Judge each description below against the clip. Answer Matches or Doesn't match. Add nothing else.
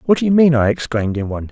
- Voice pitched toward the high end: Doesn't match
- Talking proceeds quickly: Matches